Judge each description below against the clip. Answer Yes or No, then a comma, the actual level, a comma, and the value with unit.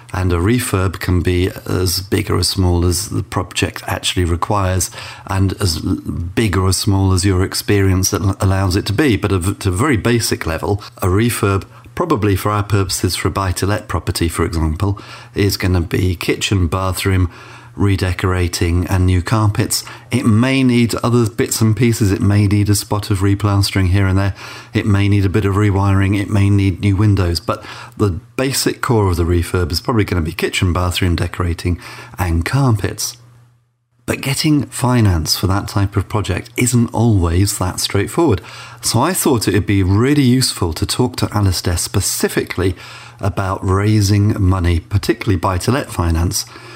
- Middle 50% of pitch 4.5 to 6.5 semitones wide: No, average, 3.3 semitones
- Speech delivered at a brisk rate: No, average, 175 wpm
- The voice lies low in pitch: Yes, low, 100 Hz